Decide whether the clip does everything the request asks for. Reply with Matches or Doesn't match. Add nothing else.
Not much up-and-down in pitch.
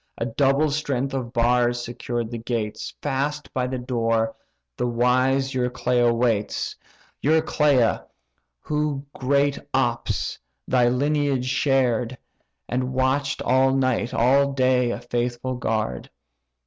Matches